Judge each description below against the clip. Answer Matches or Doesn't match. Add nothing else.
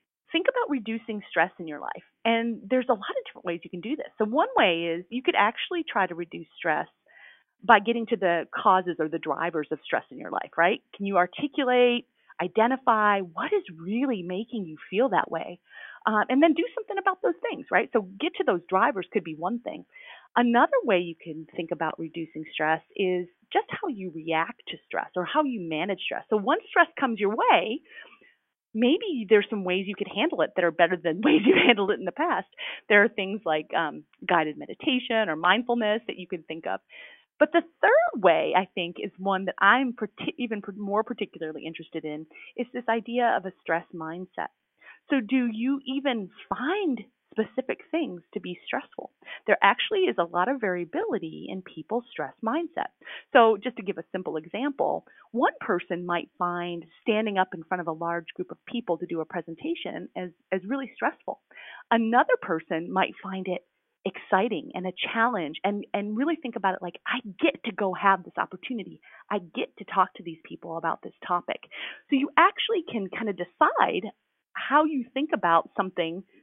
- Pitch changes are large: Matches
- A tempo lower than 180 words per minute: Doesn't match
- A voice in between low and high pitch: Doesn't match